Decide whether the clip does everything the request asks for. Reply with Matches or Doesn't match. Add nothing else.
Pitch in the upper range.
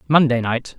Doesn't match